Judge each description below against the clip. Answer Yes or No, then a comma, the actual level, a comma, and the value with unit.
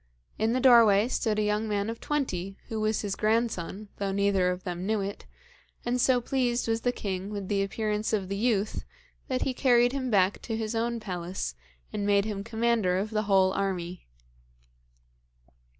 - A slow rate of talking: No, average, 180 wpm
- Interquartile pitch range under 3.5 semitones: Yes, average, 2.9 semitones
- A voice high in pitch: Yes, high, 210 Hz